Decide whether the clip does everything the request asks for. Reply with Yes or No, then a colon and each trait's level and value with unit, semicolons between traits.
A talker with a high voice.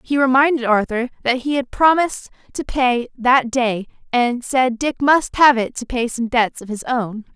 Yes: very high, 250 Hz